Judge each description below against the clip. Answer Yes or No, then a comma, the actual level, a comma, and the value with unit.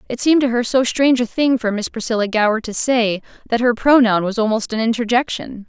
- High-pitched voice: Yes, high, 235 Hz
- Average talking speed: No, fast, 220 wpm